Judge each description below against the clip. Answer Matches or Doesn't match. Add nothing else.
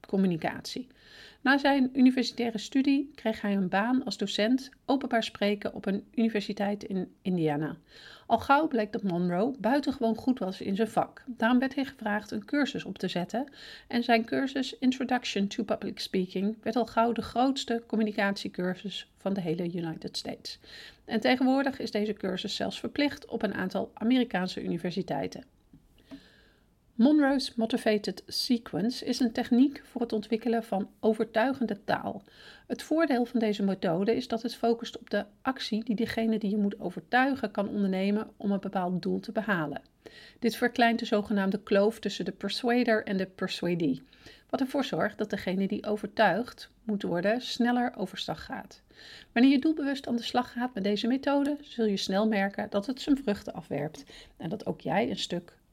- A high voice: Matches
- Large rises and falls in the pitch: Doesn't match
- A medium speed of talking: Matches